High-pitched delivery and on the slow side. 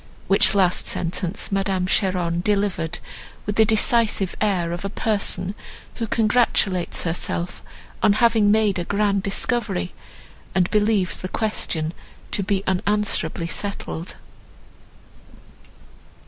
Yes: high, 195 Hz; slow, 110 wpm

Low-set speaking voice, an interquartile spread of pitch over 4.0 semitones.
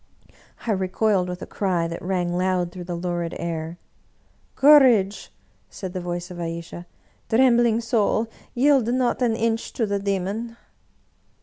No: high, 190 Hz; average, 4.6 semitones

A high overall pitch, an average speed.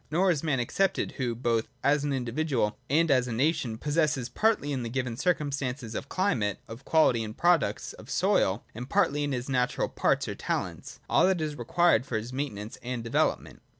No: low, 135 Hz; average, 190 wpm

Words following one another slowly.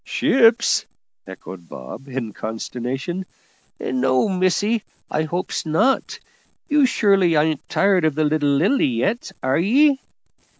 Yes: slow, 120 wpm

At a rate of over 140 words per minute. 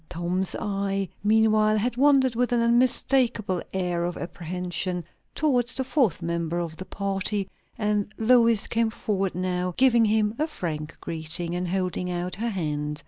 Yes: average, 150 wpm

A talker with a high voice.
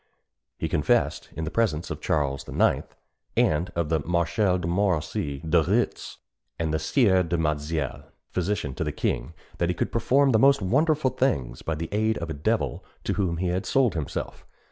No: very low, 85 Hz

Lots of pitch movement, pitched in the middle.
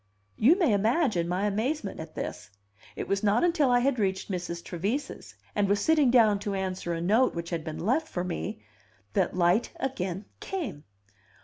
No: wide, 6.2 semitones; high, 200 Hz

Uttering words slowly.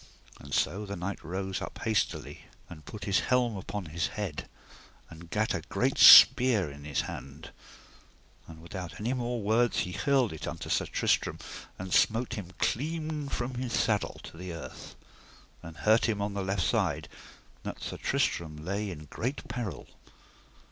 No: average, 160 wpm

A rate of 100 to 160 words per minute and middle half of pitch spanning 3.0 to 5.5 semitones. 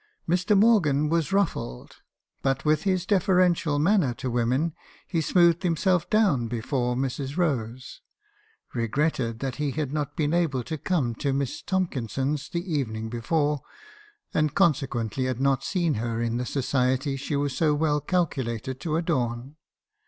Yes: average, 150 wpm; average, 4.9 semitones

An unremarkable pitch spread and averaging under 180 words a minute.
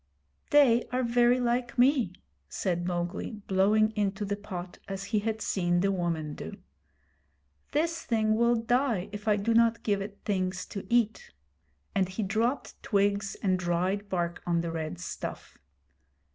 Yes: average, 4.0 semitones; average, 155 wpm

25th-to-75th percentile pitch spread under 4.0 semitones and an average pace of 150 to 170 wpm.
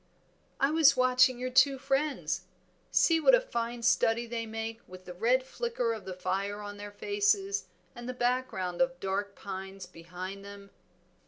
No: average, 4.9 semitones; average, 165 wpm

